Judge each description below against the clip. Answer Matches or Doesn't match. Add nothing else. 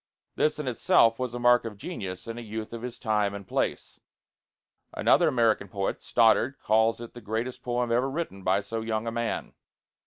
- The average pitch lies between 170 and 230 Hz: Doesn't match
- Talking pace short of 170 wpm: Doesn't match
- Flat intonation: Matches